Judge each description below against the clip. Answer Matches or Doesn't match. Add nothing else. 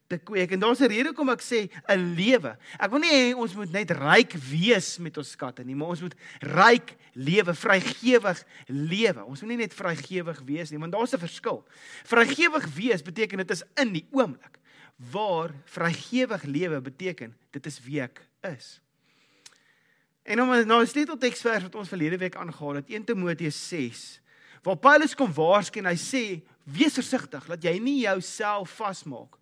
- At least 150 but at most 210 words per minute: Matches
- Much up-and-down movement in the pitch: Matches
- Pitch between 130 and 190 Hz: Matches